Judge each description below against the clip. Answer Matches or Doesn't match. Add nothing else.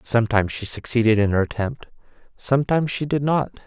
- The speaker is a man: Matches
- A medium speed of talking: Matches